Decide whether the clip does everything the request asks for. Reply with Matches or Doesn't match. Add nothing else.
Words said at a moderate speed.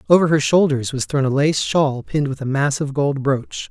Doesn't match